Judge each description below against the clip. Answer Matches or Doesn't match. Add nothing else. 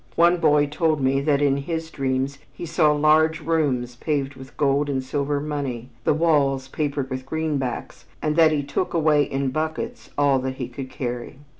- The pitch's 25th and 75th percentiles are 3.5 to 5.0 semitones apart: Doesn't match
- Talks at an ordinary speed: Matches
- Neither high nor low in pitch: Matches